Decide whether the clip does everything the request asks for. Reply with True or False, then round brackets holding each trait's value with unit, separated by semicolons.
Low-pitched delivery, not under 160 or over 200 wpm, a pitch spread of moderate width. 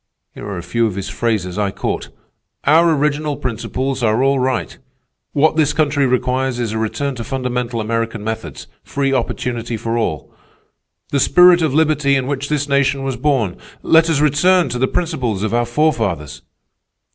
True (130 Hz; 170 wpm; 4.2 semitones)